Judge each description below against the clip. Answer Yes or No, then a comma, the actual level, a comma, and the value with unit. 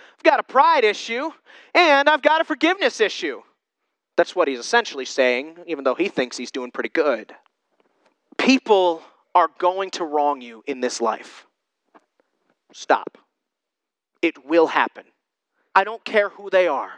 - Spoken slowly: No, average, 150 wpm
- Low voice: No, medium, 180 Hz